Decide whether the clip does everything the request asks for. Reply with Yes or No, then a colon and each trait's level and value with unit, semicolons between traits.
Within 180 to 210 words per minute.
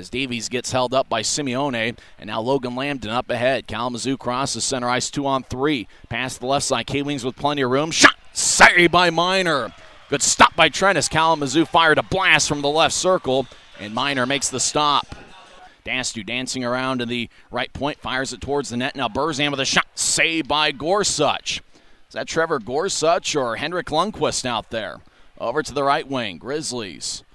Yes: average, 190 wpm